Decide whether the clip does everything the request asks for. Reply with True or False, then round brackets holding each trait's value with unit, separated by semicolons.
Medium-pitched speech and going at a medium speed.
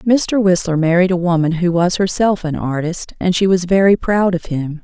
False (180 Hz; 210 wpm)